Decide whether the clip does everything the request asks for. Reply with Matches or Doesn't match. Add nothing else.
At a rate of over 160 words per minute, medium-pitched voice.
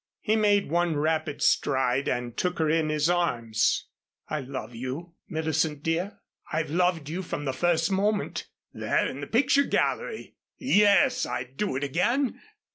Doesn't match